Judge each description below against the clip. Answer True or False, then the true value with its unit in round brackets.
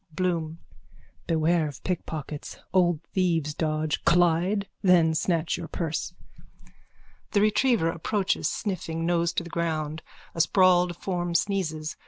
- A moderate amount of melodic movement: False (2.2 semitones)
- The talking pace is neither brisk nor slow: False (125 wpm)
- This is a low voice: False (170 Hz)